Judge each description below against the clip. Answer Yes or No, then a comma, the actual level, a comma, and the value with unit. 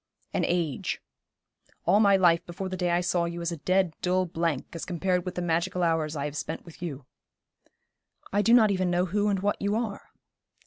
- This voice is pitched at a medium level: Yes, medium, 175 Hz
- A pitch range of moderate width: No, narrow, 2.3 semitones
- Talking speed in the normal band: No, fast, 210 wpm